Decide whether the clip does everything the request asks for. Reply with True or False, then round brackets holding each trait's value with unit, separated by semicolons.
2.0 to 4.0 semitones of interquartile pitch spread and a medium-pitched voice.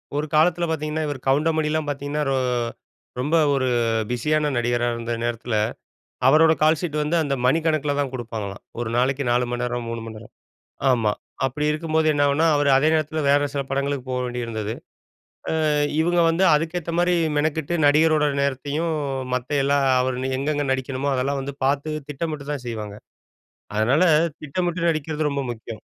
True (3.7 semitones; 145 Hz)